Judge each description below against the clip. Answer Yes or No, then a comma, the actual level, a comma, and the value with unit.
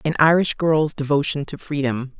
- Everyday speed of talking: Yes, average, 165 wpm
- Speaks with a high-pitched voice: No, medium, 150 Hz